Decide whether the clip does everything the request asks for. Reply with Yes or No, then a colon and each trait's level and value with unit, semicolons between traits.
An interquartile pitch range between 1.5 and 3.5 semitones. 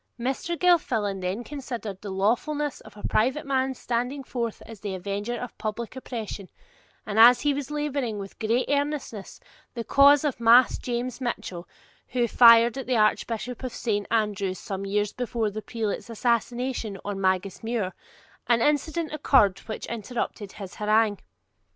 No: average, 3.9 semitones